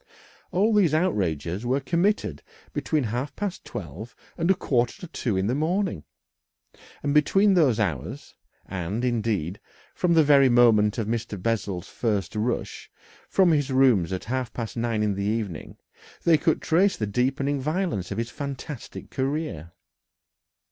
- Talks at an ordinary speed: Yes, average, 150 wpm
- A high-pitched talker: No, low, 125 Hz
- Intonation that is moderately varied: No, wide, 6.7 semitones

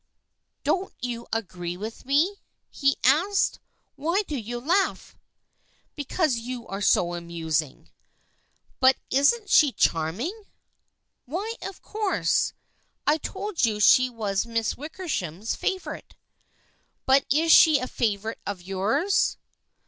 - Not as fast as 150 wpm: Yes, average, 140 wpm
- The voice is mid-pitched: No, very high, 255 Hz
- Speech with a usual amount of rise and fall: No, wide, 7.9 semitones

